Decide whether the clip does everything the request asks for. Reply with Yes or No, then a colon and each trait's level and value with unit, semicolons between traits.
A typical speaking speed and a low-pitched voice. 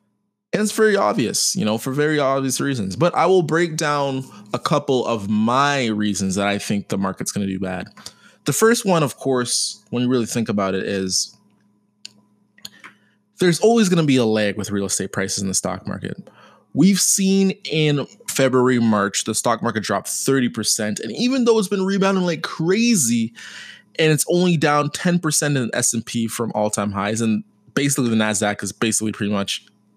Yes: average, 185 wpm; low, 120 Hz